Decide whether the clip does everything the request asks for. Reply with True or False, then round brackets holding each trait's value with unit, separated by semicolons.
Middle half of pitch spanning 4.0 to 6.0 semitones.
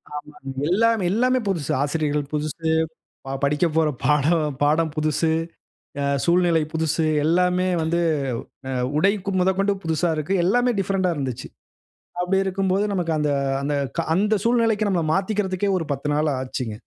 True (4.3 semitones)